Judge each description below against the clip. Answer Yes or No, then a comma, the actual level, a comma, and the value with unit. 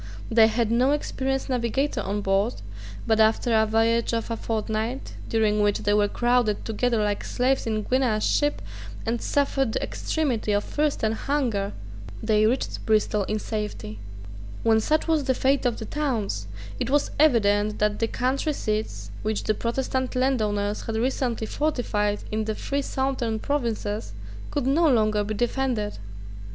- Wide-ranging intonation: No, average, 3.7 semitones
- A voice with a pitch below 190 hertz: No, high, 225 Hz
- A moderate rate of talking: Yes, average, 160 wpm